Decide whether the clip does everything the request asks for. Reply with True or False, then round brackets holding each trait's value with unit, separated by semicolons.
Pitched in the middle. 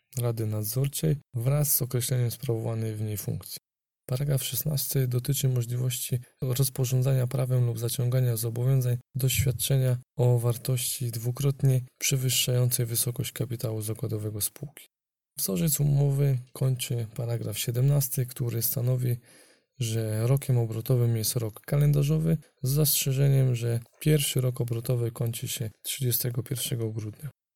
False (125 Hz)